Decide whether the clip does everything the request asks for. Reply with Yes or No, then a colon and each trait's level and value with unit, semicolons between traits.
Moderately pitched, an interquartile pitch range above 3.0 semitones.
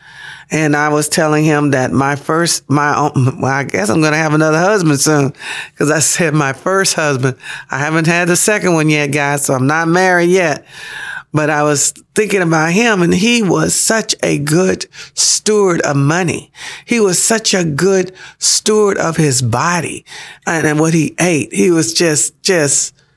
Yes: medium, 155 Hz; average, 3.8 semitones